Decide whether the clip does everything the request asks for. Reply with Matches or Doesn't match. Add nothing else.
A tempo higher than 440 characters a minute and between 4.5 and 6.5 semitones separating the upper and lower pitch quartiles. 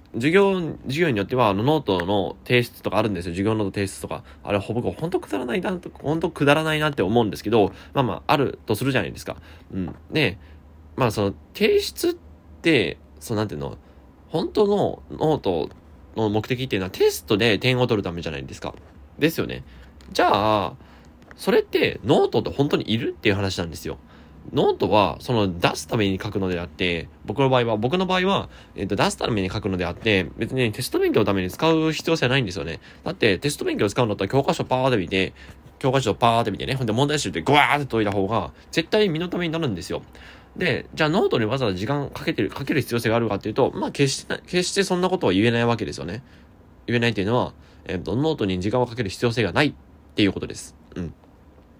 Doesn't match